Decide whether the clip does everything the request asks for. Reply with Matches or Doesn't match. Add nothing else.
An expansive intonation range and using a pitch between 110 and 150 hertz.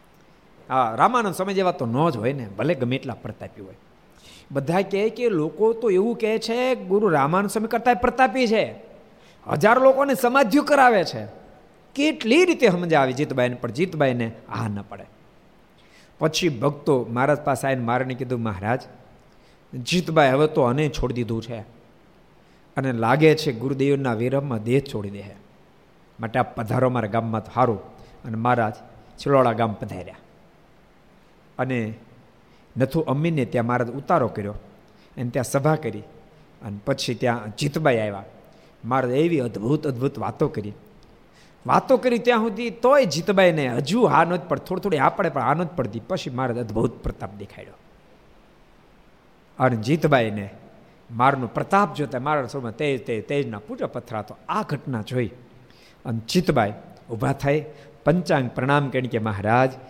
Matches